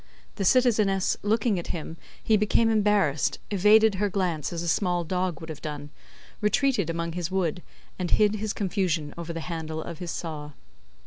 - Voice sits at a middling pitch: Yes, medium, 180 Hz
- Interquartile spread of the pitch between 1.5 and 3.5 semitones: No, average, 4.1 semitones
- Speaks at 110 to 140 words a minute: No, average, 175 wpm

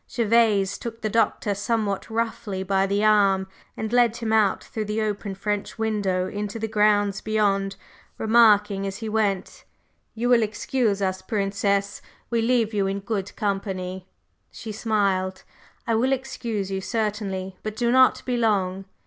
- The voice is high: Yes, high, 210 Hz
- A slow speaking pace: No, average, 155 wpm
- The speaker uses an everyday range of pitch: No, narrow, 2.2 semitones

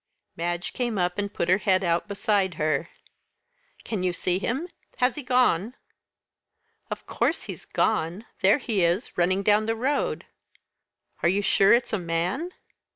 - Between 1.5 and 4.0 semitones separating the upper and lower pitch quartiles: No, average, 4.4 semitones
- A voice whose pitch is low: No, high, 195 Hz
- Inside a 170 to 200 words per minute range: No, average, 155 wpm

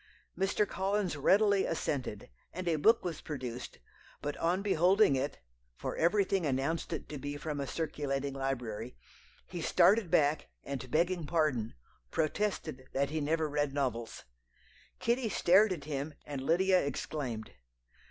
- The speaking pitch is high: No, medium, 155 Hz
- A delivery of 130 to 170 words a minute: Yes, average, 140 wpm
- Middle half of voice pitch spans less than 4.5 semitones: No, average, 5.1 semitones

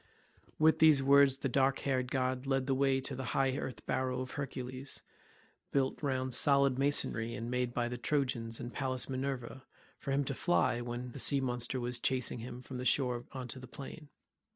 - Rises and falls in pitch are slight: Yes, narrow, 1.7 semitones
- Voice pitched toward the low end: Yes, low, 130 Hz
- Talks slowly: No, average, 200 wpm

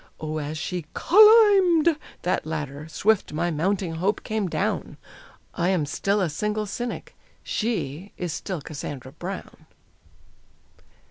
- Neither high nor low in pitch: Yes, medium, 180 Hz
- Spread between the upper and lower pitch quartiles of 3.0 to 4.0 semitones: No, average, 5.3 semitones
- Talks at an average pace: No, slow, 130 wpm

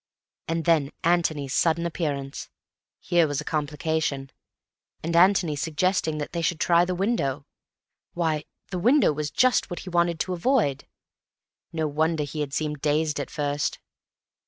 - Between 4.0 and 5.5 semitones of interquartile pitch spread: No, average, 2.8 semitones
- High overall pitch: No, medium, 160 Hz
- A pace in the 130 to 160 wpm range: Yes, average, 150 wpm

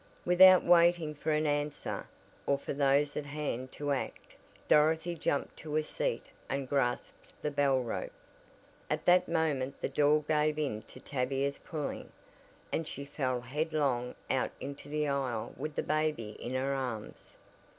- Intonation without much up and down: Yes, narrow, 2.3 semitones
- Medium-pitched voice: Yes, medium, 145 Hz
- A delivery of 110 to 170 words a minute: Yes, average, 155 wpm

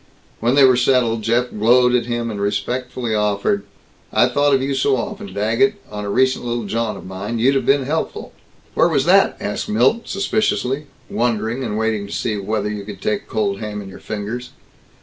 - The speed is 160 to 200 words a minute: Yes, average, 195 wpm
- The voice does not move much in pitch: No, average, 3.7 semitones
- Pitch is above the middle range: No, low, 115 Hz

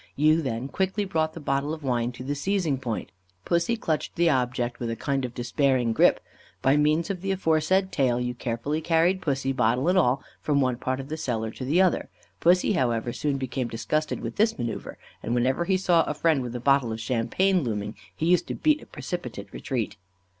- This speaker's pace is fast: Yes, fast, 210 wpm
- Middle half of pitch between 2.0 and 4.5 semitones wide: No, average, 5.3 semitones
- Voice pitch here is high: No, medium, 140 Hz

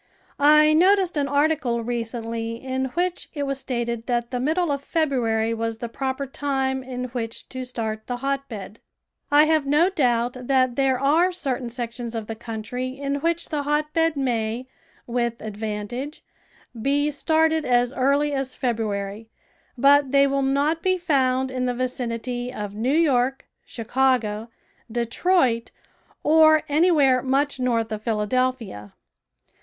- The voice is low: No, very high, 260 Hz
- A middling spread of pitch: Yes, average, 3.5 semitones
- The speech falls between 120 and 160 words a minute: Yes, average, 140 wpm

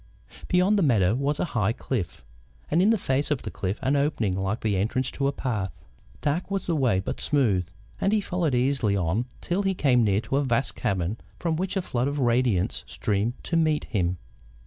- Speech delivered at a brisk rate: Yes, fast, 210 wpm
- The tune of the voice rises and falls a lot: Yes, wide, 6.8 semitones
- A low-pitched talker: Yes, low, 130 Hz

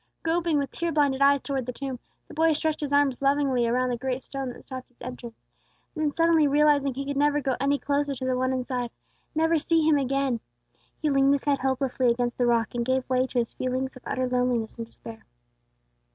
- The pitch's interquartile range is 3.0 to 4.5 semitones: No, narrow, 2.4 semitones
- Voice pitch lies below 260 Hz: No, very high, 270 Hz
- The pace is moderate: No, fast, 220 wpm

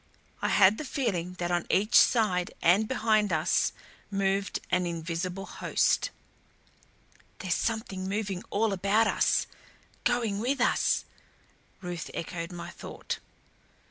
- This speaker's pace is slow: Yes, slow, 120 wpm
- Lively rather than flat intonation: No, average, 3.7 semitones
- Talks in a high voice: Yes, high, 195 Hz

